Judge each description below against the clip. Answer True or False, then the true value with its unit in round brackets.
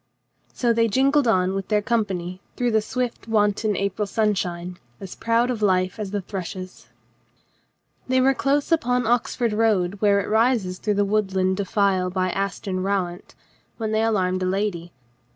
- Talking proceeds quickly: False (165 wpm)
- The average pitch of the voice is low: False (205 Hz)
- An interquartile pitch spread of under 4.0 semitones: True (3.4 semitones)